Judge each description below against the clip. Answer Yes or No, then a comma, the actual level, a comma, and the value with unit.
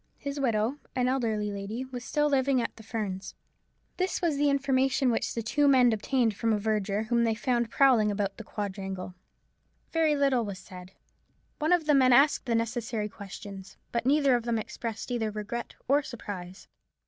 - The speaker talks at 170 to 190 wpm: Yes, average, 180 wpm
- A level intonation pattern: No, average, 4.2 semitones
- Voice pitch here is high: Yes, high, 235 Hz